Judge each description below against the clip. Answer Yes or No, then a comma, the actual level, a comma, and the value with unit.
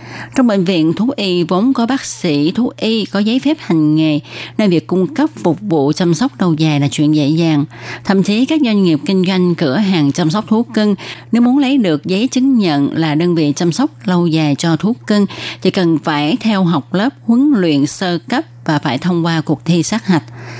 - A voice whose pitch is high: No, medium, 175 Hz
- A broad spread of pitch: Yes, wide, 5.9 semitones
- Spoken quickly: No, average, 225 wpm